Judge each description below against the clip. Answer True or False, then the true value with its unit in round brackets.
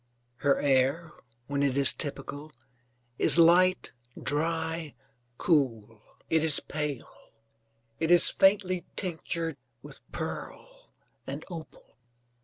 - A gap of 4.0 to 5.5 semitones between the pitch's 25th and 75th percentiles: False (3.2 semitones)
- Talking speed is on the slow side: True (100 wpm)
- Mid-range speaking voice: True (160 Hz)